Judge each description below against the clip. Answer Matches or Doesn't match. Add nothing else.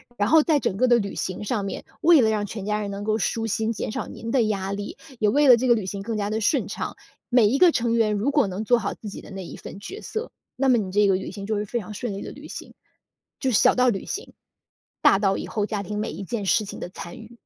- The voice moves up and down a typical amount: Matches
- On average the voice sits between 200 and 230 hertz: Matches